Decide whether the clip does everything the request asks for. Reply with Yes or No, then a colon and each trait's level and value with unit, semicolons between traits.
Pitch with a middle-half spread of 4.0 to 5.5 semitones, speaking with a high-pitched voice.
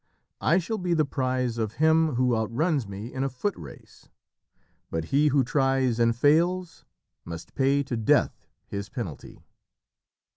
No: average, 5.0 semitones; low, 130 Hz